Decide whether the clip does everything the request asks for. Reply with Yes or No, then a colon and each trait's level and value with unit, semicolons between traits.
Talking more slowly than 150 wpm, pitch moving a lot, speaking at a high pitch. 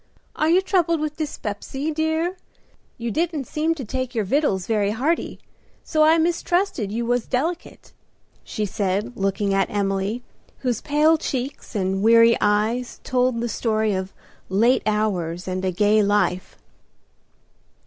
Yes: average, 140 wpm; wide, 6.9 semitones; high, 235 Hz